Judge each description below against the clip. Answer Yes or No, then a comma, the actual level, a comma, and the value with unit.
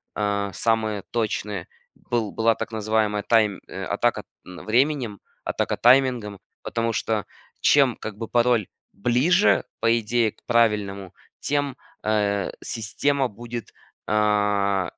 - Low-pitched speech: Yes, low, 110 Hz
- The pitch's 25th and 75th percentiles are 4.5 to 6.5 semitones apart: No, narrow, 2.6 semitones